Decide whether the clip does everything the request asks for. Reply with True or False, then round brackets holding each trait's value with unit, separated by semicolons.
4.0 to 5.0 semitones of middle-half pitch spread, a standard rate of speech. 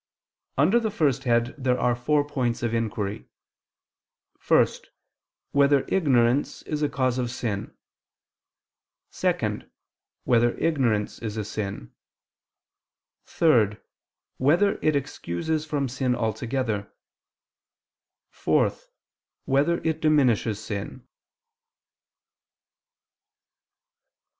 False (4.4 semitones; 90 wpm)